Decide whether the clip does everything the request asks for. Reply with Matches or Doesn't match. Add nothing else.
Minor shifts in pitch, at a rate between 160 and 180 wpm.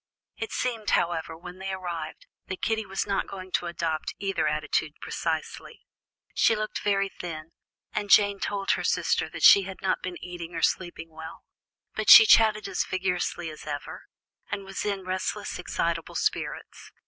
Doesn't match